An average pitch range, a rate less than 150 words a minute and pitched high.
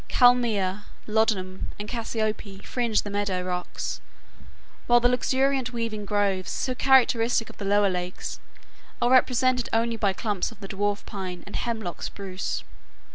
Yes: average, 3.5 semitones; average, 140 wpm; high, 215 Hz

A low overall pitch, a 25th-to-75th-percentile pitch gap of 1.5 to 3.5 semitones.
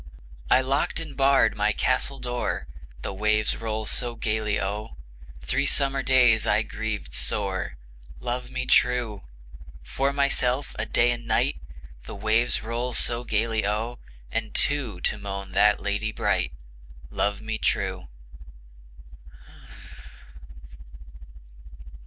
Yes: low, 115 Hz; average, 3.1 semitones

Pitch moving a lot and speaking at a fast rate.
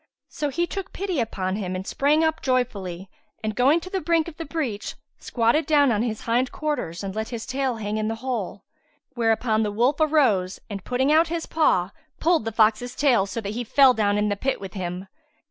Yes: wide, 6.1 semitones; fast, 215 wpm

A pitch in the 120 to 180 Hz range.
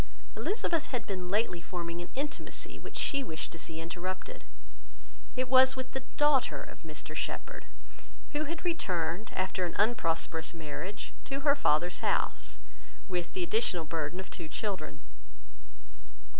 No: high, 190 Hz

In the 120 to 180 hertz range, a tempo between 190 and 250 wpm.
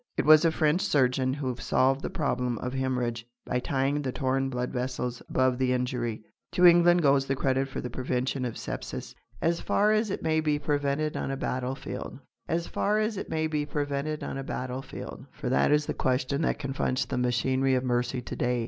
Yes: low, 135 Hz; average, 200 wpm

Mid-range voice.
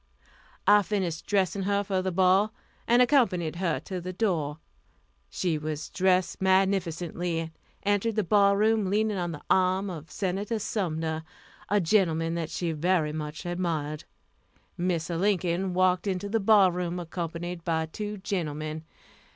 Yes: medium, 180 Hz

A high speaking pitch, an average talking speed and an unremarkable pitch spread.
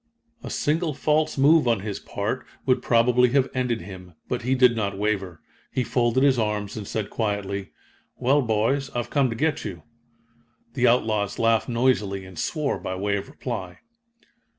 No: low, 115 Hz; average, 170 wpm; average, 4.2 semitones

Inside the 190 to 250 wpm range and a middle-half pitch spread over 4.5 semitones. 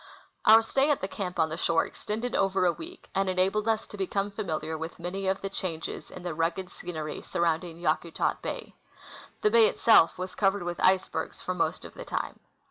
No: average, 200 wpm; average, 3.4 semitones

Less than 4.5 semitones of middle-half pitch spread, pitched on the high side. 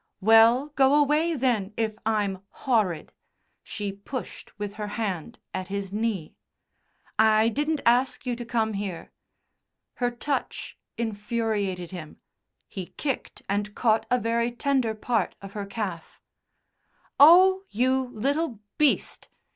Yes: average, 4.1 semitones; high, 225 Hz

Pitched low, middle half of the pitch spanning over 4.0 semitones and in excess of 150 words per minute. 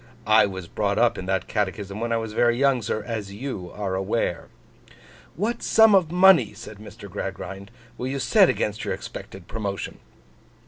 Yes: low, 110 Hz; average, 4.7 semitones; average, 175 wpm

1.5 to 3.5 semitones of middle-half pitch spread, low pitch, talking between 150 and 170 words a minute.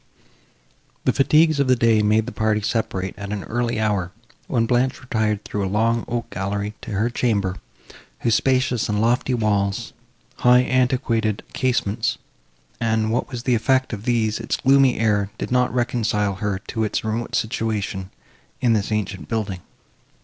Yes: average, 2.9 semitones; low, 110 Hz; average, 160 wpm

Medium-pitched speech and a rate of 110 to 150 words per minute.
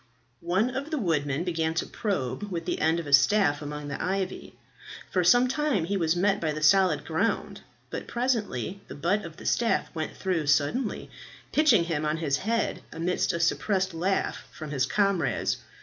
No: medium, 175 Hz; average, 180 wpm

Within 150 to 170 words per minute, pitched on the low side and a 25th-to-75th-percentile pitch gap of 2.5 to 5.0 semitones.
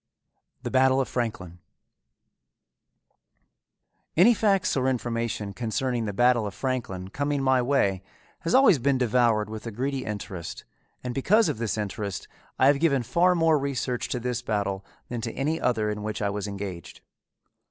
Yes: average, 160 wpm; low, 120 Hz; average, 4.4 semitones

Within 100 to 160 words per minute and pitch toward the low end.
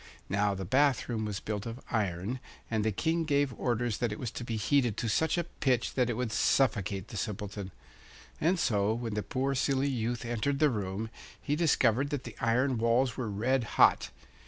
No: average, 200 wpm; low, 120 Hz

